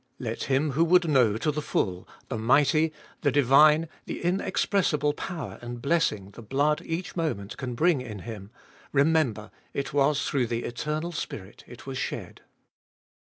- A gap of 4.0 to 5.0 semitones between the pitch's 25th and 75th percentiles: Yes, average, 4.7 semitones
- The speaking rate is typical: Yes, average, 160 wpm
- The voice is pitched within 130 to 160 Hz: Yes, medium, 140 Hz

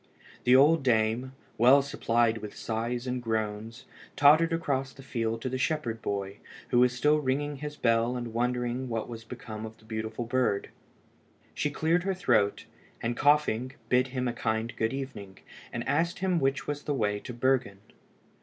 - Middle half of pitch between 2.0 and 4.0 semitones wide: Yes, average, 3.5 semitones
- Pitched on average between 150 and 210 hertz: No, low, 125 Hz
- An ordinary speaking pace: Yes, average, 175 wpm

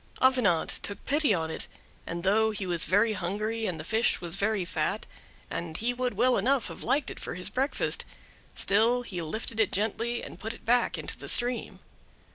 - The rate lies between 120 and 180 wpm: No, average, 195 wpm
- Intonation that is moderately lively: Yes, average, 4.7 semitones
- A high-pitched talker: Yes, high, 220 Hz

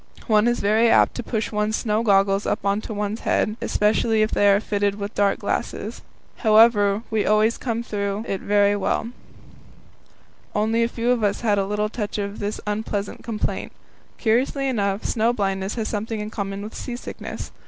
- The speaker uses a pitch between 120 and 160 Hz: No, high, 210 Hz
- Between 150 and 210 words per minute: Yes, average, 180 wpm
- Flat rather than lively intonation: Yes, narrow, 1.8 semitones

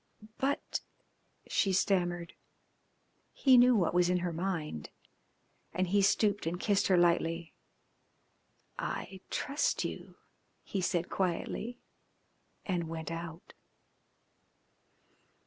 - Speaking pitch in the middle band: Yes, medium, 180 Hz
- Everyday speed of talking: No, slow, 105 wpm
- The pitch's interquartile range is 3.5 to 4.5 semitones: No, average, 2.7 semitones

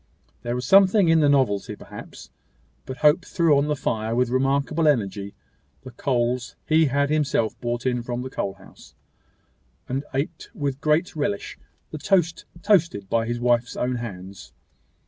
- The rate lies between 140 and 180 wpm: Yes, average, 160 wpm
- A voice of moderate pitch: No, low, 130 Hz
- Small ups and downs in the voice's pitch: No, average, 4.3 semitones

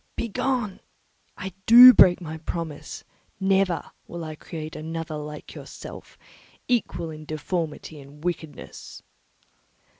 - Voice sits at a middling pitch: Yes, medium, 165 Hz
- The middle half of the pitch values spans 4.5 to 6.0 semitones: No, average, 3.7 semitones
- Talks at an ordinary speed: No, slow, 110 wpm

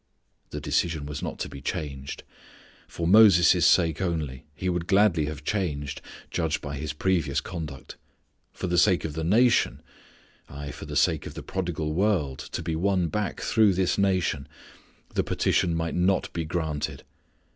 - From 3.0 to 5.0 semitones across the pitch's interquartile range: Yes, average, 3.8 semitones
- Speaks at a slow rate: No, average, 165 wpm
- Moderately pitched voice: No, very low, 80 Hz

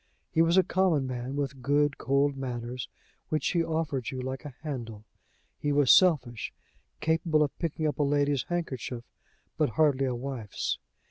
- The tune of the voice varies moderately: Yes, average, 3.5 semitones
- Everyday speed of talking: Yes, average, 160 wpm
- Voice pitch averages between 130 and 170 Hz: Yes, medium, 140 Hz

